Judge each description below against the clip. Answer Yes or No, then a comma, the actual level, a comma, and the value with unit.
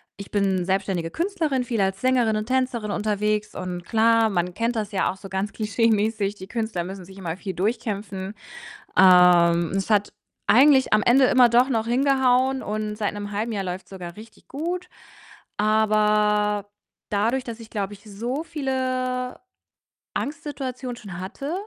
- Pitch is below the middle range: No, high, 215 Hz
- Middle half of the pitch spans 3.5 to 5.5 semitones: Yes, average, 4.2 semitones